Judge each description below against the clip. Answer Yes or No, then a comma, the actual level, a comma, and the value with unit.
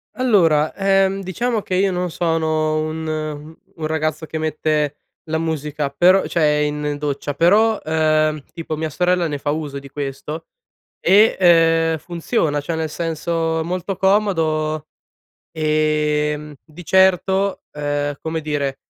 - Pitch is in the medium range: Yes, medium, 160 Hz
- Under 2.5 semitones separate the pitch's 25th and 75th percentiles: No, average, 2.8 semitones